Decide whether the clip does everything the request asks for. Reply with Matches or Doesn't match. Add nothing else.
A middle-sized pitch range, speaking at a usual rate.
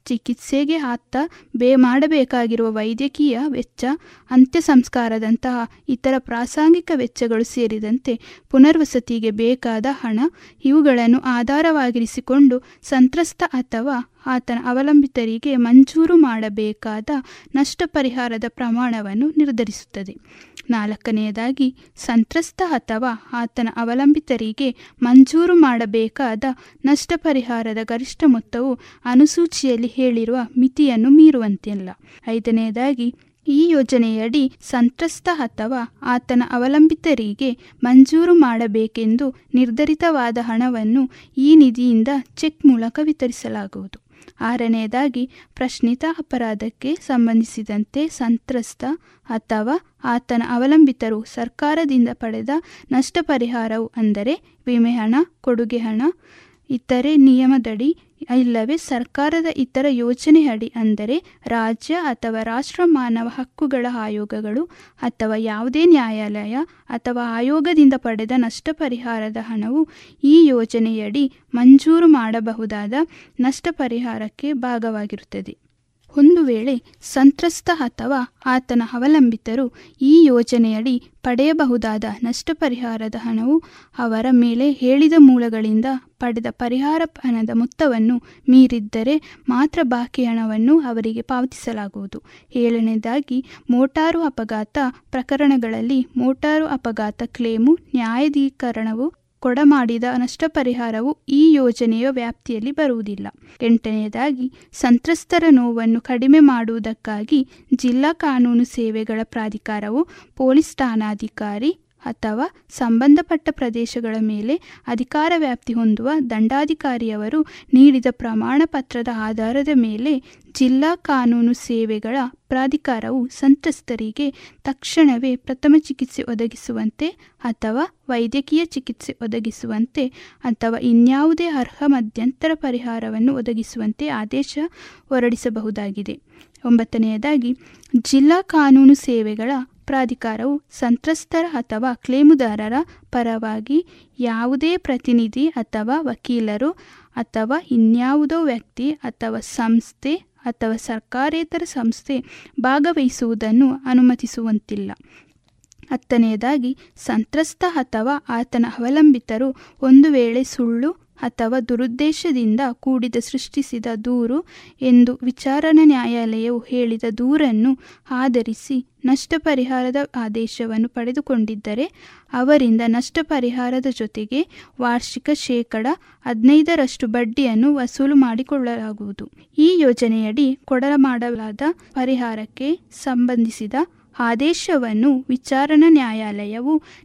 Matches